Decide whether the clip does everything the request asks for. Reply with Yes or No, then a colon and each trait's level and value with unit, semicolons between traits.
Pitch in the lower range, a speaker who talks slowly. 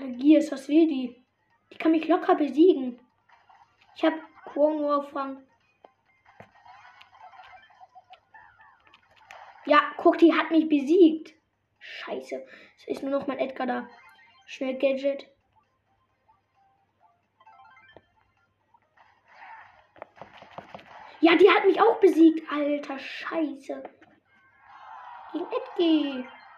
No: very high, 315 Hz; slow, 85 wpm